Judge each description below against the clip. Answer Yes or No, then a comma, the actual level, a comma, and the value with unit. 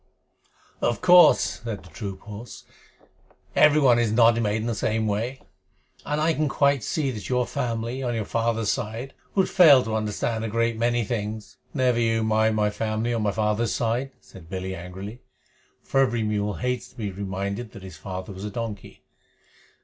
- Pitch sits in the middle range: No, low, 115 Hz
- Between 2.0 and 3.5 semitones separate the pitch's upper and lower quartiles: Yes, average, 2.7 semitones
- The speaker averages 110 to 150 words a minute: No, average, 180 wpm